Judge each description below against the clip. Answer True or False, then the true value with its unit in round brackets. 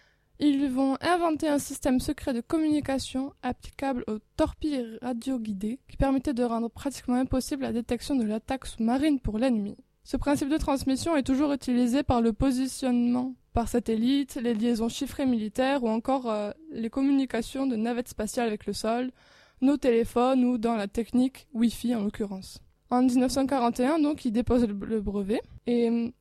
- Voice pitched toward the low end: False (250 Hz)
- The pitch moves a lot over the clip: False (2.8 semitones)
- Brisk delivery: False (160 wpm)